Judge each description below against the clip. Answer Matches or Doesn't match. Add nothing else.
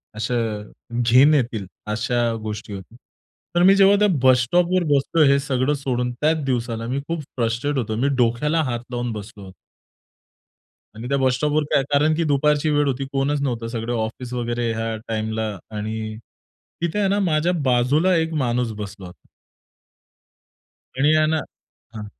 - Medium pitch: Doesn't match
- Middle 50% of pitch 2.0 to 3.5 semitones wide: Doesn't match